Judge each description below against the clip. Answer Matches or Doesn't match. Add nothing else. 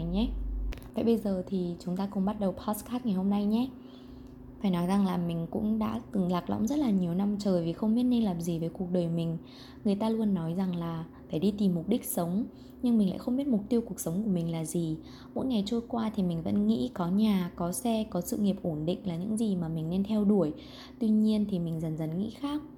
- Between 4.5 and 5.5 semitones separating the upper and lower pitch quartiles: Doesn't match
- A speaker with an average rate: Doesn't match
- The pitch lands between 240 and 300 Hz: Doesn't match